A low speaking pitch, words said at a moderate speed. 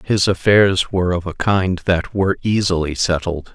Yes: very low, 90 Hz; average, 170 wpm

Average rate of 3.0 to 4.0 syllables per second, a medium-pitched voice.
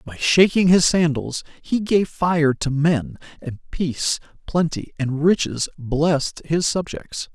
Yes: 3.8 syllables/s; medium, 155 Hz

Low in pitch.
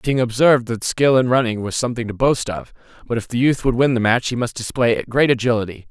Yes: low, 120 Hz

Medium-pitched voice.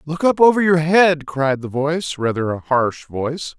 Yes: medium, 150 Hz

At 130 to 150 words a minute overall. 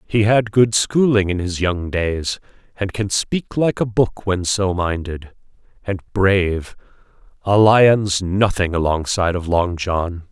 Yes: average, 145 wpm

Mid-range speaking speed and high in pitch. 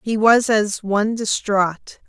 Yes: average, 145 wpm; high, 210 Hz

